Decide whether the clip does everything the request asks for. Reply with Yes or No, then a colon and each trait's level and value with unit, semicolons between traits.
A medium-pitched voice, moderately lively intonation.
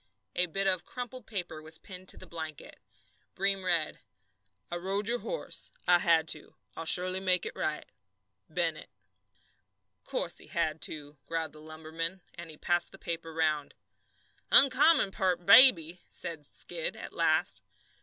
Yes: medium, 175 Hz; average, 3.3 semitones